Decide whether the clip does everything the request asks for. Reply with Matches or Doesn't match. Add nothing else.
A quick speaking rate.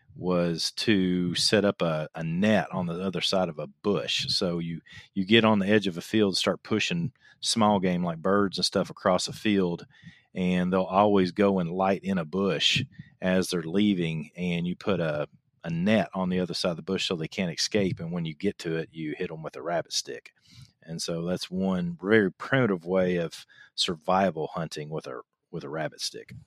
Matches